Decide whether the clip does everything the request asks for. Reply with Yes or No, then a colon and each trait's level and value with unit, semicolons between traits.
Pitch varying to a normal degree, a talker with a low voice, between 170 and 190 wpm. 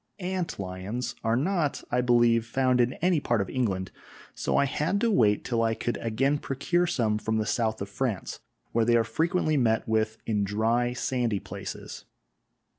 Yes: average, 3.7 semitones; low, 120 Hz; average, 180 wpm